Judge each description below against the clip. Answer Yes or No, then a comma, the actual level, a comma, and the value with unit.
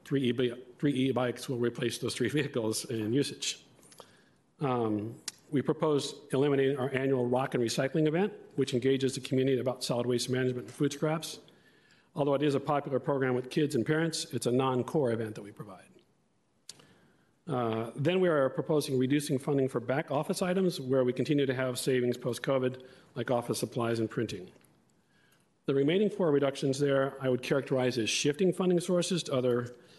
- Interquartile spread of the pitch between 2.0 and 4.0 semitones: Yes, average, 3.0 semitones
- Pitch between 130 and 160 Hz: Yes, low, 135 Hz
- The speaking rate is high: No, average, 175 wpm